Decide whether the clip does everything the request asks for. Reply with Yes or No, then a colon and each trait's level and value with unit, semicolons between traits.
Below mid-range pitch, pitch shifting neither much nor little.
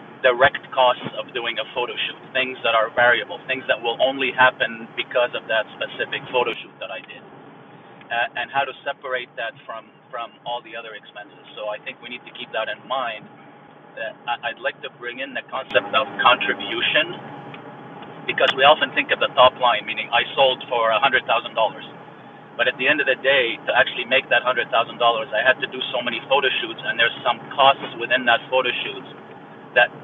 No: low, 125 Hz; narrow, 2.0 semitones